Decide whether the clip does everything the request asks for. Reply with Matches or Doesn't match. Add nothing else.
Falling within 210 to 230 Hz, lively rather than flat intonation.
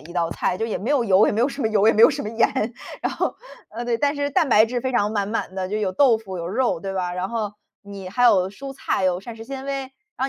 Doesn't match